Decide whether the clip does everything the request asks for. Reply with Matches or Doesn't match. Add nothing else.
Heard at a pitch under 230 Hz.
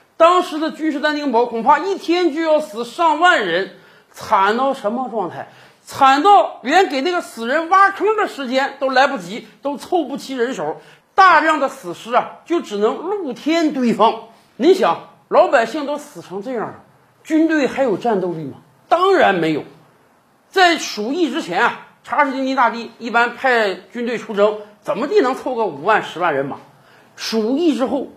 Doesn't match